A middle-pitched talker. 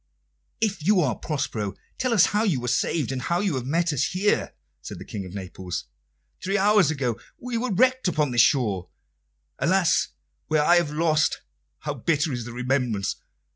Yes: medium, 150 Hz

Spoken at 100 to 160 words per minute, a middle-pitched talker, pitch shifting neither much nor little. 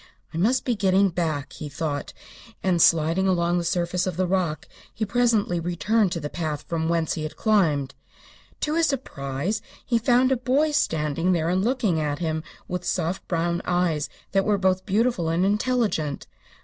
No: average, 175 wpm; medium, 180 Hz; average, 4.8 semitones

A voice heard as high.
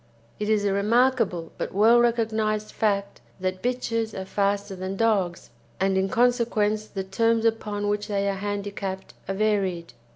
Yes: high, 205 Hz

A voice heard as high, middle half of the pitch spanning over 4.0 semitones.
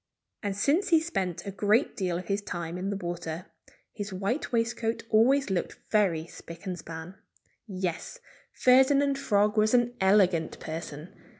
Yes: high, 200 Hz; average, 5.0 semitones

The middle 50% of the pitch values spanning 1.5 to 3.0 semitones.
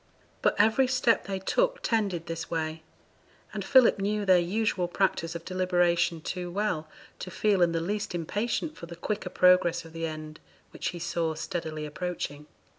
No: average, 3.7 semitones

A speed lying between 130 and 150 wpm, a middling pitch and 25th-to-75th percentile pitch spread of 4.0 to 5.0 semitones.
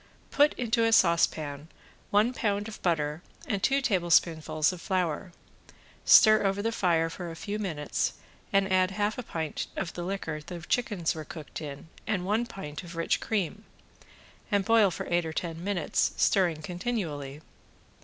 No: average, 165 wpm; medium, 180 Hz; average, 4.4 semitones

